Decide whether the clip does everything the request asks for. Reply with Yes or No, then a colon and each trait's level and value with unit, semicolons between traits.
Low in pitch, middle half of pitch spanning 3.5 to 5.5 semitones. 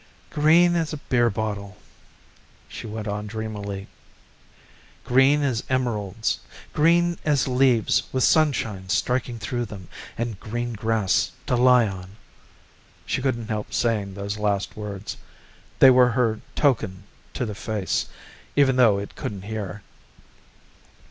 Yes: low, 110 Hz; average, 3.9 semitones